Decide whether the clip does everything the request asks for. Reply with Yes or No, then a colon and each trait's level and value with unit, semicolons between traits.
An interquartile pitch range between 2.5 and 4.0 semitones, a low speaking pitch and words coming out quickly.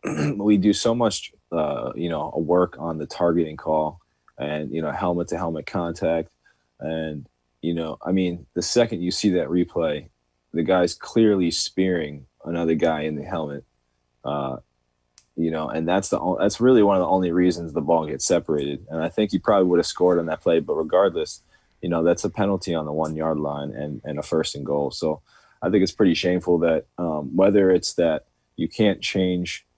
No: average, 3.3 semitones; very low, 80 Hz; average, 195 wpm